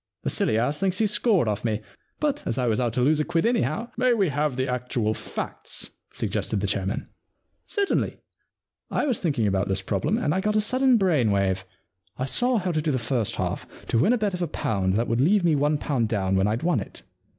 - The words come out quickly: Yes, fast, 250 wpm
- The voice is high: No, medium, 140 Hz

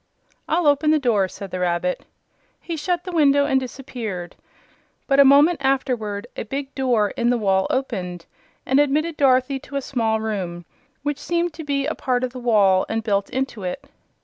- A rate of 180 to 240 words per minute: Yes, average, 185 wpm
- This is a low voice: No, very high, 255 Hz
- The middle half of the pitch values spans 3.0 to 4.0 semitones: No, wide, 5.4 semitones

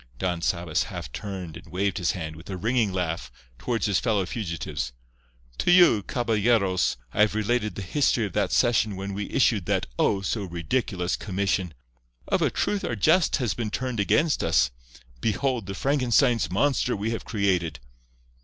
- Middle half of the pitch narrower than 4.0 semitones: No, average, 4.6 semitones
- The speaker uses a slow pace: No, average, 170 wpm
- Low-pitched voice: Yes, low, 100 Hz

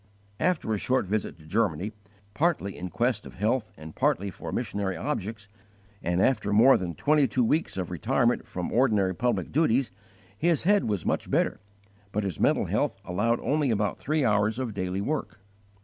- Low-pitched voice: Yes, low, 110 Hz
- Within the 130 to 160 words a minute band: No, average, 175 wpm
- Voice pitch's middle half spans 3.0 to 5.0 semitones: No, wide, 5.4 semitones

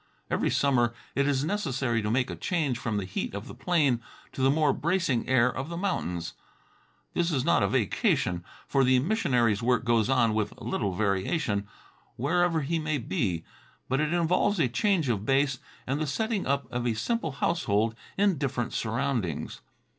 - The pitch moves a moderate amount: No, wide, 5.7 semitones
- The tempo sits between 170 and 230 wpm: Yes, average, 175 wpm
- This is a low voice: Yes, low, 130 Hz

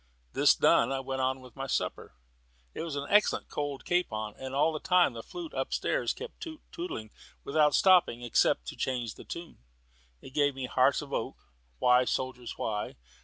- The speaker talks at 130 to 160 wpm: No, average, 185 wpm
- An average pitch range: Yes, average, 4.8 semitones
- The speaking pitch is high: No, low, 135 Hz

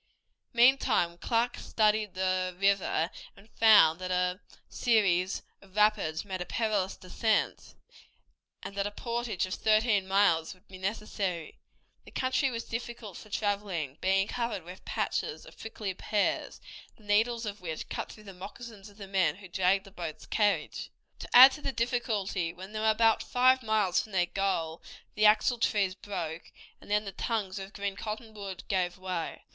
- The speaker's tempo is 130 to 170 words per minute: Yes, average, 165 wpm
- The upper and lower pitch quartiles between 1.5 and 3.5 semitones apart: Yes, average, 2.9 semitones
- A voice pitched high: Yes, high, 200 Hz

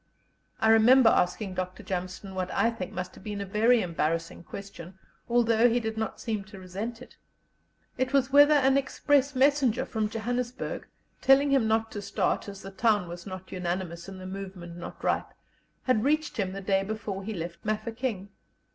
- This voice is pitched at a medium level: No, high, 210 Hz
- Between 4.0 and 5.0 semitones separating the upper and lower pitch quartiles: Yes, average, 4.5 semitones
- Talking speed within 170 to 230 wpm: Yes, average, 180 wpm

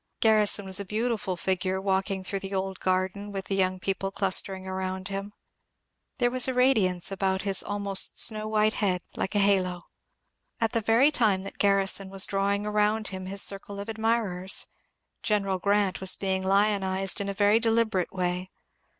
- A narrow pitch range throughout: Yes, narrow, 1.8 semitones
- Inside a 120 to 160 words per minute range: No, average, 175 wpm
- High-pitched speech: Yes, high, 195 Hz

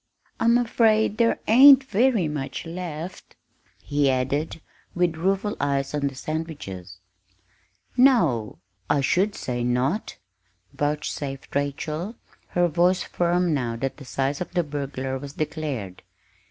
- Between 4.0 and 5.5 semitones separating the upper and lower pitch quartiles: Yes, average, 5.2 semitones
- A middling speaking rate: No, slow, 125 wpm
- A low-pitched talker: No, medium, 155 Hz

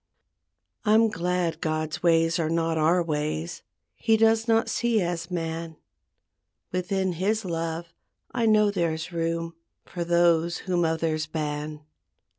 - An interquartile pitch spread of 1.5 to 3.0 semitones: Yes, narrow, 2.5 semitones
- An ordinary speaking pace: No, slow, 125 wpm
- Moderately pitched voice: Yes, medium, 170 Hz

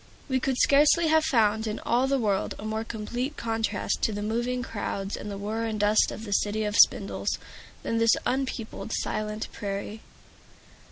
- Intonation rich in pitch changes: No, average, 2.9 semitones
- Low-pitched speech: No, high, 220 Hz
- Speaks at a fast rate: No, average, 175 wpm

